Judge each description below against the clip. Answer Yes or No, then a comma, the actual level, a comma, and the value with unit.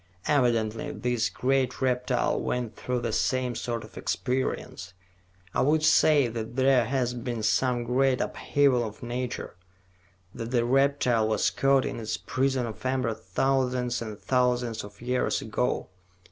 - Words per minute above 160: No, average, 145 wpm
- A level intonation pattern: Yes, narrow, 2.1 semitones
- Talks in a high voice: No, low, 125 Hz